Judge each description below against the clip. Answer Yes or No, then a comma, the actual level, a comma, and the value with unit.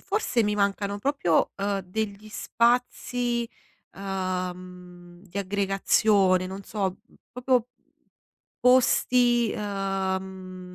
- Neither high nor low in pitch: No, high, 200 Hz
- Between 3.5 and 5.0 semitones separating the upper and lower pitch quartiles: Yes, average, 4.1 semitones